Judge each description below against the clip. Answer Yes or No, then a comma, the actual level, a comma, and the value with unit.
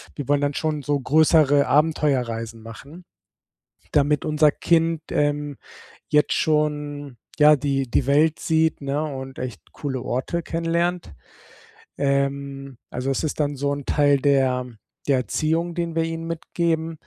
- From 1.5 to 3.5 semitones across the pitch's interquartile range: Yes, narrow, 2.5 semitones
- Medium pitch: Yes, medium, 145 Hz